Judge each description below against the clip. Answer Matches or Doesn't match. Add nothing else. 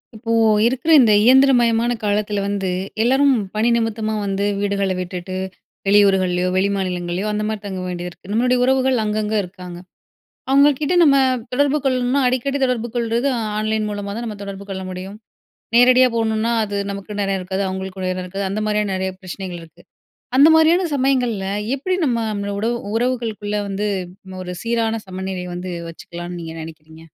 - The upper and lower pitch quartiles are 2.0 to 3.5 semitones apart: Doesn't match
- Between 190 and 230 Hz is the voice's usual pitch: Matches